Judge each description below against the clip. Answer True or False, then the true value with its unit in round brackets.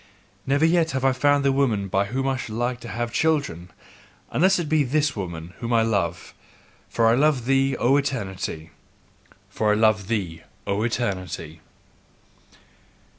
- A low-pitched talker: True (120 Hz)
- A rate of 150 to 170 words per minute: True (160 wpm)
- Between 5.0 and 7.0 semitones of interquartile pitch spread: True (5.6 semitones)